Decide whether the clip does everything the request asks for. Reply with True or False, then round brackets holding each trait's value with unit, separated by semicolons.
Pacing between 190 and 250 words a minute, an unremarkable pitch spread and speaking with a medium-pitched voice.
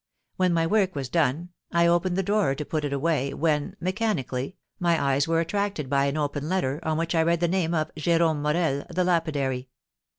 True (200 wpm; 3.4 semitones; 165 Hz)